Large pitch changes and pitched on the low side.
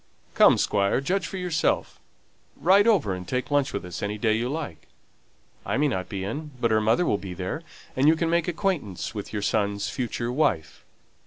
Yes: wide, 7.8 semitones; low, 120 Hz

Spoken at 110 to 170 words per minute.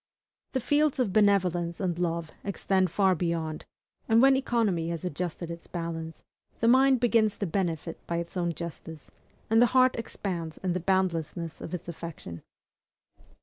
Yes: average, 155 wpm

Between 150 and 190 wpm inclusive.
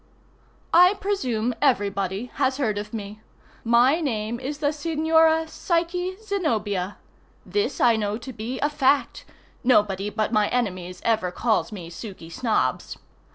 No: average, 140 wpm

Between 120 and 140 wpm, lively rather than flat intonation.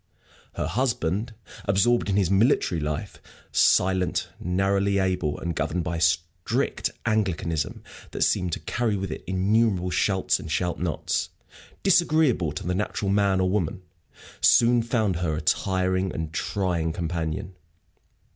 No: slow, 135 wpm; average, 3.3 semitones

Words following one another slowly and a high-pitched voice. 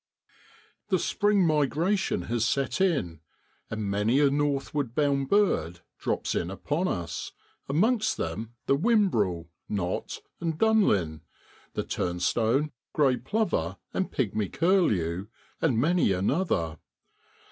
No: slow, 115 wpm; low, 135 Hz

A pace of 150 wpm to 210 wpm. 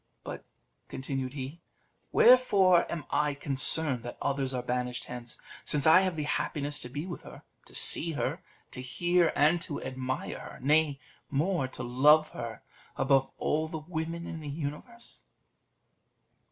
Yes: average, 155 wpm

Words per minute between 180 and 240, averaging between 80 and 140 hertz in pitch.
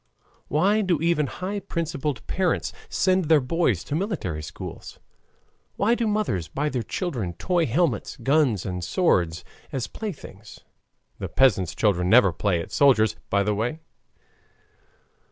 No: slow, 135 wpm; low, 135 Hz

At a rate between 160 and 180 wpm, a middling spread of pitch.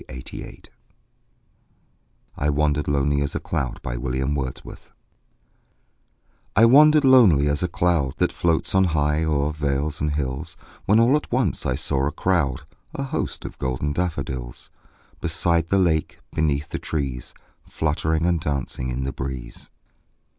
No: average, 140 wpm; average, 3.7 semitones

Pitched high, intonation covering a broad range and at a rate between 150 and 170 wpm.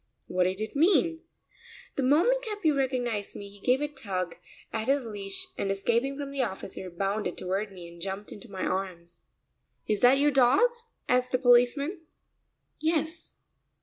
Yes: high, 245 Hz; wide, 6.4 semitones; average, 160 wpm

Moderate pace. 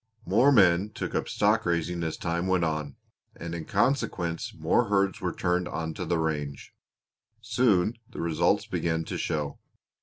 Yes: average, 155 wpm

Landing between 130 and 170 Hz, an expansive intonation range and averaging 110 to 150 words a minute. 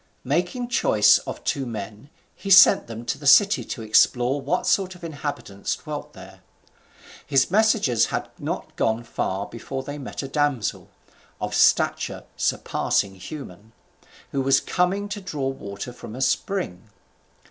Yes: low, 135 Hz; wide, 7.8 semitones; average, 145 wpm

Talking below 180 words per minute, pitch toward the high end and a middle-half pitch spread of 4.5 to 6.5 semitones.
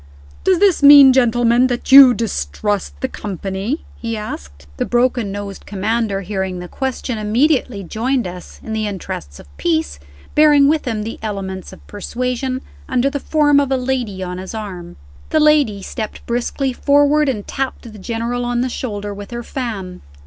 Yes: average, 170 wpm; high, 230 Hz; average, 4.9 semitones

